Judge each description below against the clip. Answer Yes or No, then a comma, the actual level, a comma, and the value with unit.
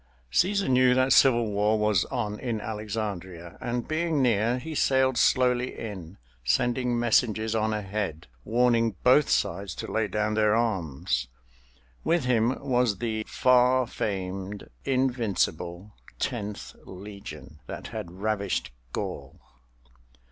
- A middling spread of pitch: Yes, average, 3.7 semitones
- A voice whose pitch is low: Yes, low, 110 Hz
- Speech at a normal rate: No, slow, 120 wpm